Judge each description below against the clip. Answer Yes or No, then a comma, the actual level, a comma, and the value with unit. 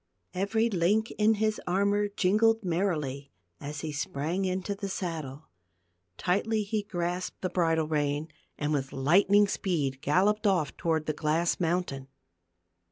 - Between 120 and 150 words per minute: Yes, average, 140 wpm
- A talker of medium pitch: Yes, medium, 180 Hz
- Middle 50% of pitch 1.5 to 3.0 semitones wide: No, average, 4.9 semitones